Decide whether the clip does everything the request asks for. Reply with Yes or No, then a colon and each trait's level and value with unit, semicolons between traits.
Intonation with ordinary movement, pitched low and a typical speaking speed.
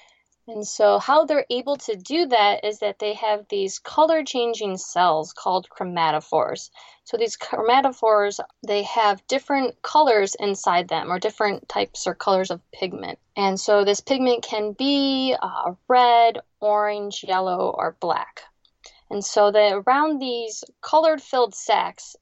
No: average, 4.6 semitones; high, 215 Hz; average, 145 wpm